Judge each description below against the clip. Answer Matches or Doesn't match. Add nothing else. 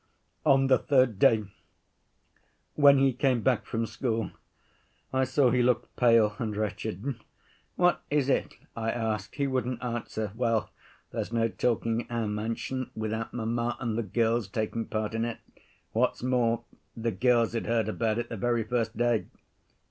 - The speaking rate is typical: Matches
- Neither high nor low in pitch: Doesn't match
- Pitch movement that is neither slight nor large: Doesn't match